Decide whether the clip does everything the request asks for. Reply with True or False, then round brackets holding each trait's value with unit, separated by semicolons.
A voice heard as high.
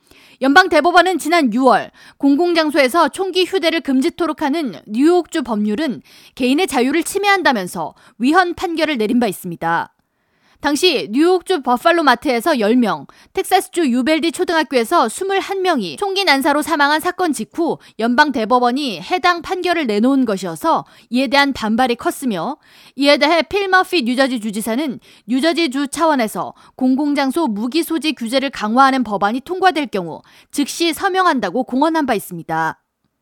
True (290 Hz)